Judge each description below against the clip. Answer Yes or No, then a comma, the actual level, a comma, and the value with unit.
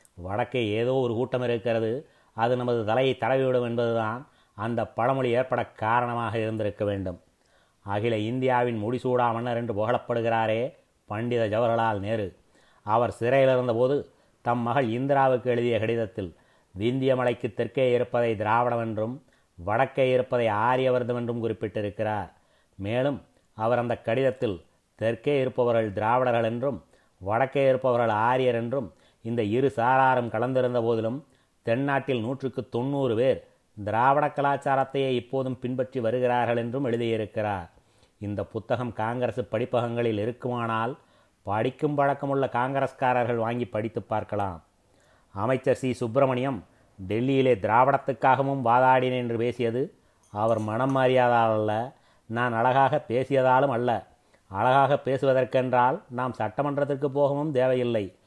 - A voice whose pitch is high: No, low, 120 Hz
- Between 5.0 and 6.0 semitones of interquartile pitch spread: No, average, 2.7 semitones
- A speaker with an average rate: Yes, average, 105 wpm